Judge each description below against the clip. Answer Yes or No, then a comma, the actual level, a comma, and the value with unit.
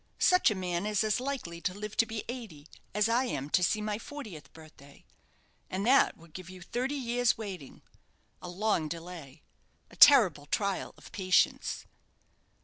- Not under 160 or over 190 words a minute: Yes, average, 165 wpm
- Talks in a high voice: Yes, high, 200 Hz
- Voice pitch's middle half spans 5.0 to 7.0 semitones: Yes, average, 5.3 semitones